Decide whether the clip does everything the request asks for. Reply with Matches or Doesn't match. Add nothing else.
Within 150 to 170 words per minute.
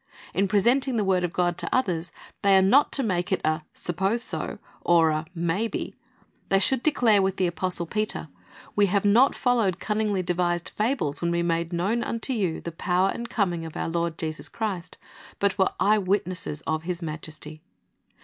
Doesn't match